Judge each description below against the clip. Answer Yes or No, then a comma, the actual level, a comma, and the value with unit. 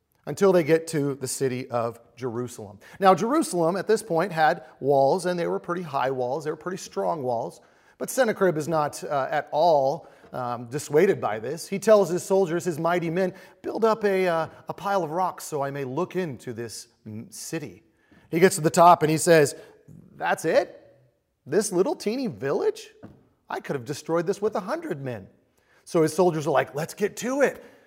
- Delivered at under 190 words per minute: No, average, 195 wpm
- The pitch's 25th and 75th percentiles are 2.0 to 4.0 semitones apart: No, wide, 5.5 semitones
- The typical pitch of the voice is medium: Yes, medium, 170 Hz